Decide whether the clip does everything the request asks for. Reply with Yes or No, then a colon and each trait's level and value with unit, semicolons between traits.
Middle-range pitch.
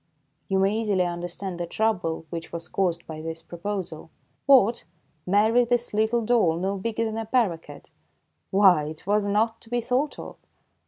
No: high, 200 Hz